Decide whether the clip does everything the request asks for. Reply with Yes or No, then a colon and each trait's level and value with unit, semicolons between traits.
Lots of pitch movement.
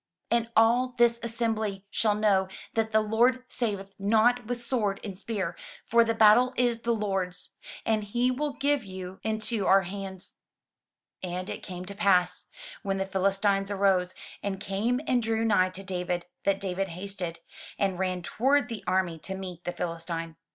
No: average, 3.5 semitones